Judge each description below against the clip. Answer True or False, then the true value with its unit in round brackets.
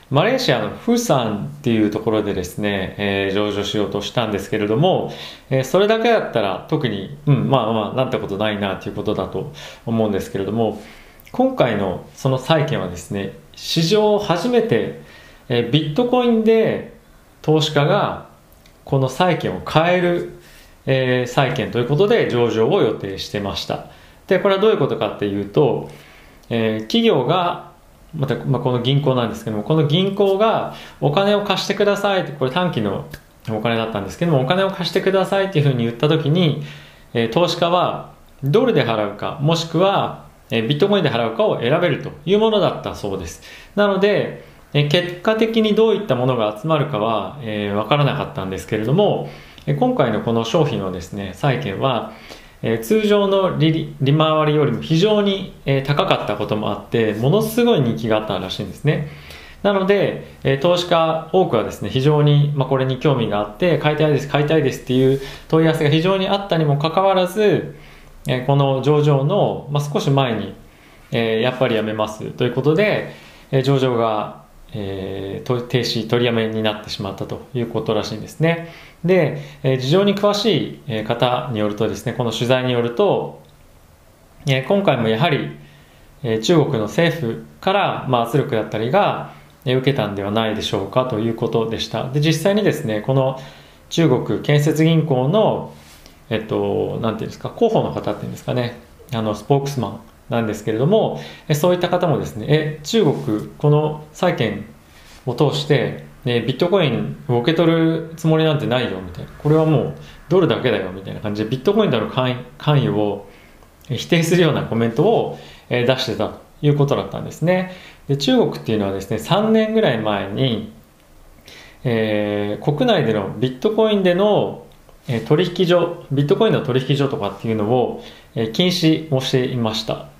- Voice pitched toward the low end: True (130 Hz)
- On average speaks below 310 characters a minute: False (345 characters per minute)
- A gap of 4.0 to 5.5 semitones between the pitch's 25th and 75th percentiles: False (7.2 semitones)